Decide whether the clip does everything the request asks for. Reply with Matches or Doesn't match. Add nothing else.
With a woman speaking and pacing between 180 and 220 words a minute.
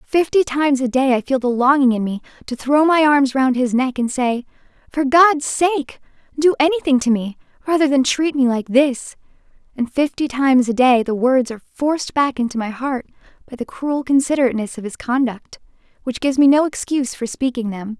Matches